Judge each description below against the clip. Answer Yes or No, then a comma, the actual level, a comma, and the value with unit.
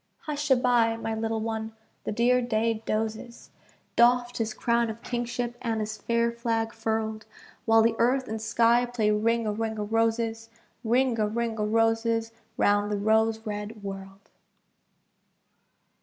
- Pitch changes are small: Yes, narrow, 1.3 semitones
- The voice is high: Yes, high, 225 Hz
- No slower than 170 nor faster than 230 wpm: No, average, 155 wpm